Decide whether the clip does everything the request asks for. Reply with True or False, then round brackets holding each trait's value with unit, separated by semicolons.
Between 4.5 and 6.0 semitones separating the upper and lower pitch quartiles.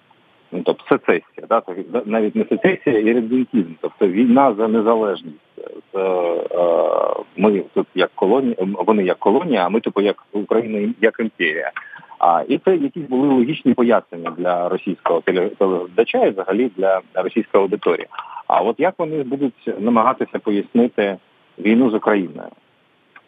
True (4.9 semitones)